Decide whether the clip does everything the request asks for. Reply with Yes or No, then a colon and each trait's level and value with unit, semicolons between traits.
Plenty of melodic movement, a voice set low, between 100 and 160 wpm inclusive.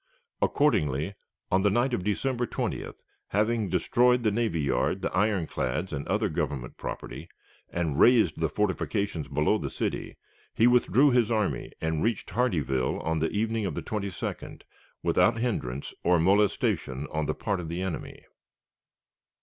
Yes: wide, 6.2 semitones; very low, 95 Hz; average, 150 wpm